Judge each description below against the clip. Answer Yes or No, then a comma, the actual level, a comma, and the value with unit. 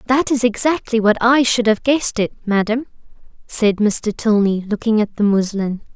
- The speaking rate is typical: Yes, average, 170 wpm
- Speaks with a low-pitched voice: No, high, 225 Hz